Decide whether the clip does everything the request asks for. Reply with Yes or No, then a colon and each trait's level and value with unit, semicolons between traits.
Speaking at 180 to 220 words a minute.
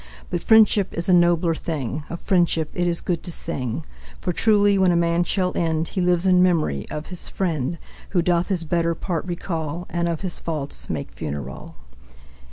Yes: average, 185 wpm